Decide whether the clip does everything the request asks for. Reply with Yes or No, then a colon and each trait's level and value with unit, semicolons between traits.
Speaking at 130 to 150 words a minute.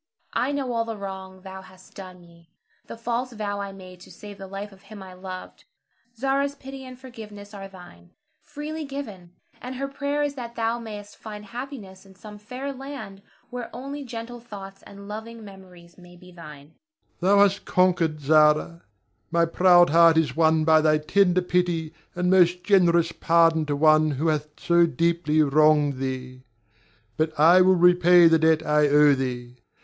No: average, 175 wpm